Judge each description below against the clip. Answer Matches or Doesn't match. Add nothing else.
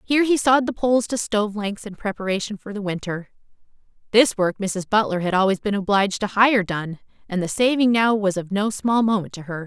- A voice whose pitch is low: Doesn't match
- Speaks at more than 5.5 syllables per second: Matches